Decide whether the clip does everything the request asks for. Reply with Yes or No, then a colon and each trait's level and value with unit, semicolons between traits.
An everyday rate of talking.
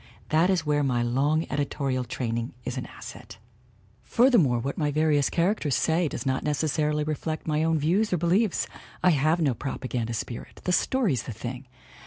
Yes: average, 170 wpm